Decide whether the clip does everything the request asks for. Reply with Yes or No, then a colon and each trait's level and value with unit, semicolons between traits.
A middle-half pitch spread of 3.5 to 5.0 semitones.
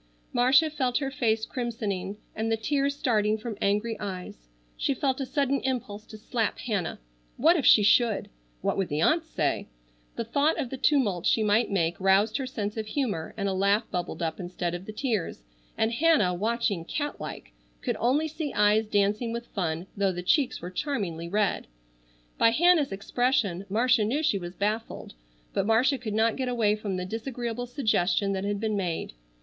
Yes: average, 4.4 semitones